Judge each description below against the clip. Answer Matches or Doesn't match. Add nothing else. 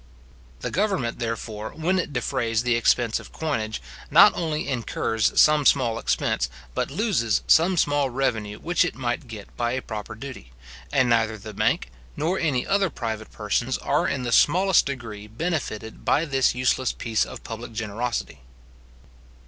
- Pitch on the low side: Matches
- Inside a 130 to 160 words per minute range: Matches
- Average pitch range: Matches